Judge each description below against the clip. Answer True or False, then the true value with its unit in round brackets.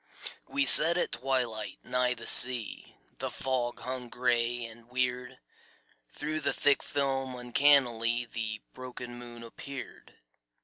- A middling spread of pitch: False (2.0 semitones)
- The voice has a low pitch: True (125 Hz)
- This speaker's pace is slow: True (125 wpm)